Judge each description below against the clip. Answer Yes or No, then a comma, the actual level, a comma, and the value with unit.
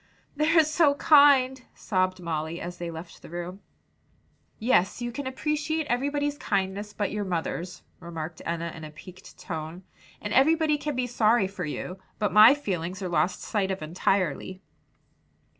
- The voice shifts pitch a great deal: Yes, wide, 7.2 semitones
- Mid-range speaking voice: No, high, 195 Hz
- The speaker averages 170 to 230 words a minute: No, average, 155 wpm